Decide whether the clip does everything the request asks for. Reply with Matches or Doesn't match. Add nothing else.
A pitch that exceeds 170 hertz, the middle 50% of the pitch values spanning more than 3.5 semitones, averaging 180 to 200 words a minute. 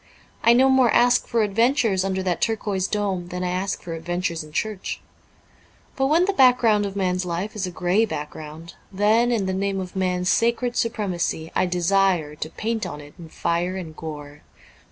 Matches